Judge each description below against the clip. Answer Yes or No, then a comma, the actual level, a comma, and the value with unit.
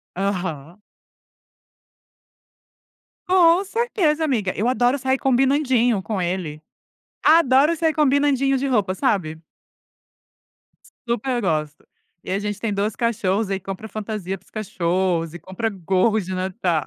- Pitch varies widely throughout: Yes, wide, 6.1 semitones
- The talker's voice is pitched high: Yes, high, 210 Hz